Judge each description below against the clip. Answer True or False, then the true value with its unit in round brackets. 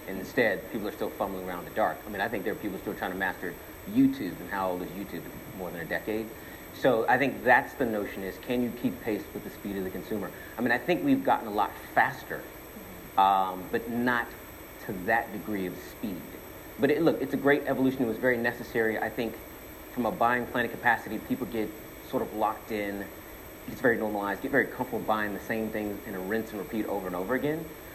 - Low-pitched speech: True (110 Hz)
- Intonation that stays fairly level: False (3.7 semitones)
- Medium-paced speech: False (230 wpm)